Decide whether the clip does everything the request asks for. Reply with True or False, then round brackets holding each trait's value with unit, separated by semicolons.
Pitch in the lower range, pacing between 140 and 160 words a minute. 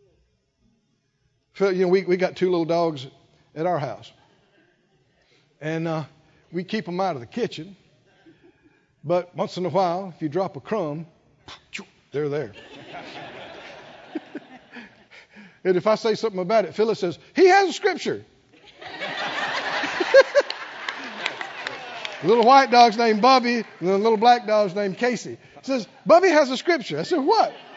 False (190 Hz; 145 wpm)